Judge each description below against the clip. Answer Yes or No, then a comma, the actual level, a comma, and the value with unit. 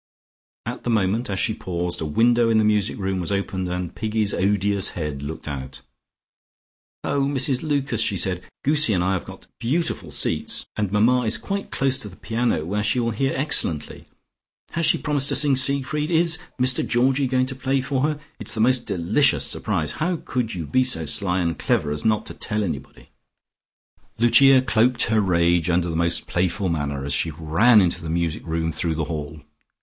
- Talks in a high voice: No, low, 105 Hz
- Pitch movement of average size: No, wide, 7.0 semitones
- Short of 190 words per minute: No, average, 195 wpm